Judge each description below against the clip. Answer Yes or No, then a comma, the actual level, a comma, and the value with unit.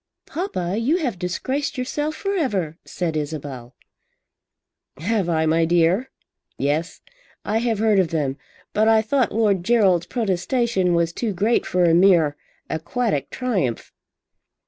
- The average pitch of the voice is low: No, high, 190 Hz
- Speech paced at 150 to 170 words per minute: No, slow, 135 wpm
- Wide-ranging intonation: Yes, wide, 6.1 semitones